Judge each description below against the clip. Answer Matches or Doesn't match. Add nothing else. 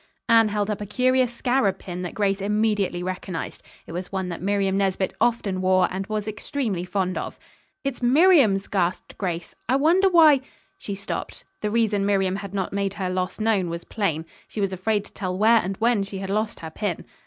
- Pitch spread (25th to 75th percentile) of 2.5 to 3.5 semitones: Matches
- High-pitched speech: Matches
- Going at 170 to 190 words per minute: Doesn't match